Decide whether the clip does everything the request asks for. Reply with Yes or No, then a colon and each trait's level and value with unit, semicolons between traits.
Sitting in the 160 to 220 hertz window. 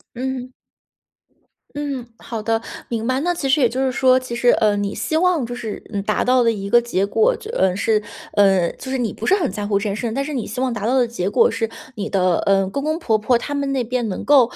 No: high, 240 Hz